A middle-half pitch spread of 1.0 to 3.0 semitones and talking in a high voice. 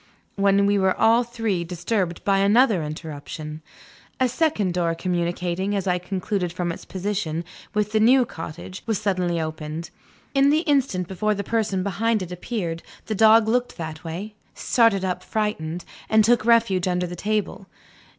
No: average, 4.0 semitones; high, 195 Hz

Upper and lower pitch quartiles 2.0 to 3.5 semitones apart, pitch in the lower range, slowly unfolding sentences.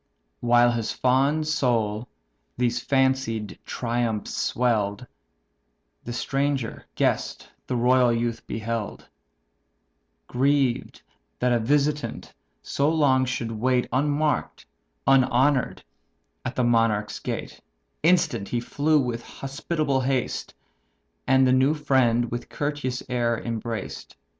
Yes: average, 2.7 semitones; low, 125 Hz; slow, 105 wpm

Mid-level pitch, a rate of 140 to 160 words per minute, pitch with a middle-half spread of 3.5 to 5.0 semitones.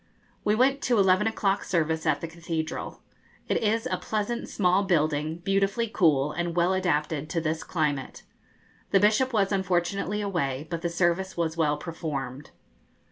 Yes: medium, 175 Hz; average, 155 wpm; average, 3.9 semitones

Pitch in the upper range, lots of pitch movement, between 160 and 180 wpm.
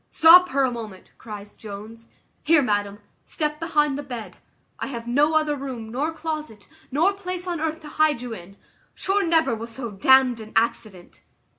Yes: very high, 265 Hz; wide, 5.9 semitones; average, 175 wpm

